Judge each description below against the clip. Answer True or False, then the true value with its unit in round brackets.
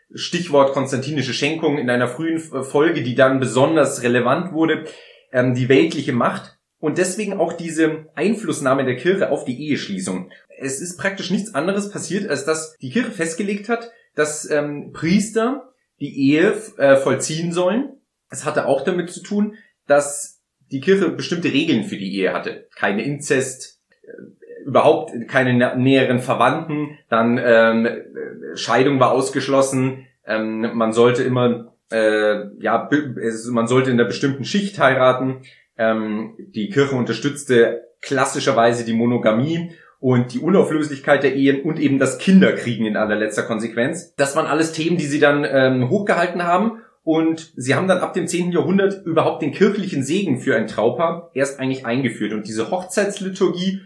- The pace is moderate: True (150 wpm)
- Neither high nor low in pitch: True (145 Hz)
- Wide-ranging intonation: True (5.8 semitones)